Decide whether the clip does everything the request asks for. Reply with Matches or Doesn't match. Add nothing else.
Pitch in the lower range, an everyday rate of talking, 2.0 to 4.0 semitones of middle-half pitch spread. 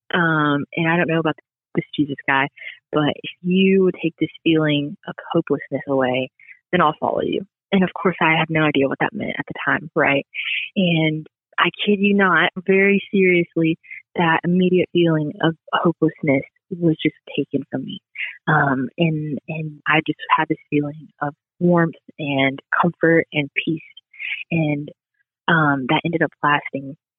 Doesn't match